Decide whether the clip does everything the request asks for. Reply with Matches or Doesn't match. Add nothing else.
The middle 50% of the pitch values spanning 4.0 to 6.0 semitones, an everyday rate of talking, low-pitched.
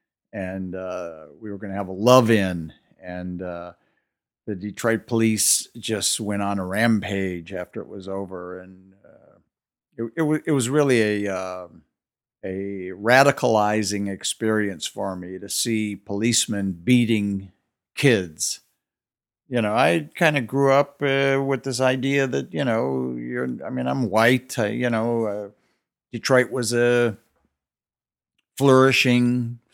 Matches